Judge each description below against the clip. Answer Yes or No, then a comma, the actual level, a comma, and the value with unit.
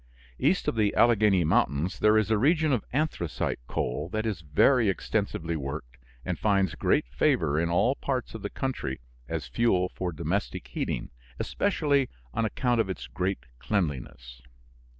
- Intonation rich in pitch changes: Yes, wide, 7.3 semitones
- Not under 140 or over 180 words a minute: Yes, average, 155 wpm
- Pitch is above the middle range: No, low, 100 Hz